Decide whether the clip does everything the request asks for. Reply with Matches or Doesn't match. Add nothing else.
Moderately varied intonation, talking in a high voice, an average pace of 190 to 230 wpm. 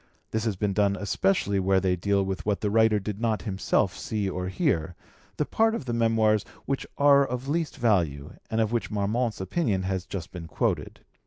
Doesn't match